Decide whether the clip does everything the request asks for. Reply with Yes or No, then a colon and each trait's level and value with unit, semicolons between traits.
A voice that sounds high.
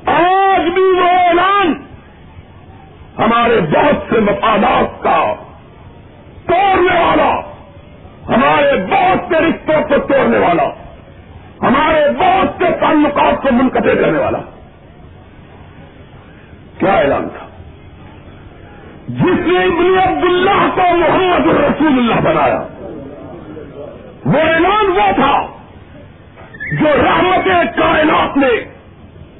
Yes: very high, 335 Hz